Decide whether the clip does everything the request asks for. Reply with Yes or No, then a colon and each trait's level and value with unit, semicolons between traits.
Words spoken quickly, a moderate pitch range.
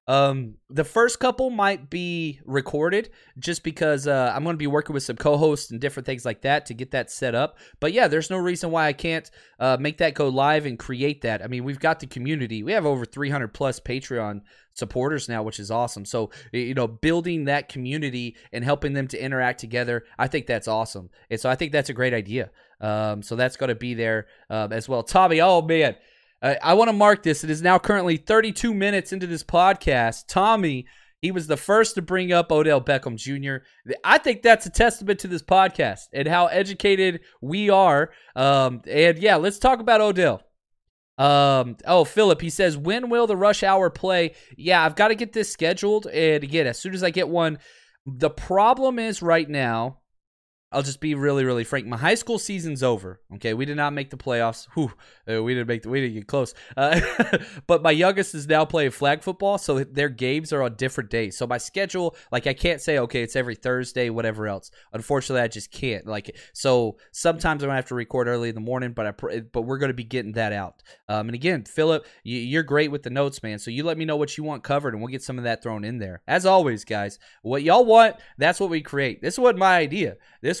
No: fast, 220 wpm; wide, 6.0 semitones